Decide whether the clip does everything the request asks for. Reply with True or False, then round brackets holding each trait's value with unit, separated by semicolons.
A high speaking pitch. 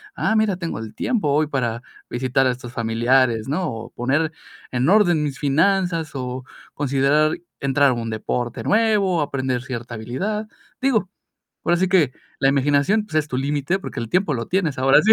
False (140 Hz)